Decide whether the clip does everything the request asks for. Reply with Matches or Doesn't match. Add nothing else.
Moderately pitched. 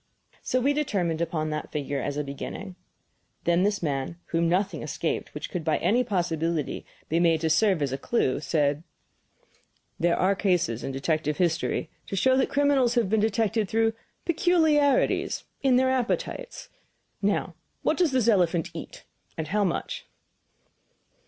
Matches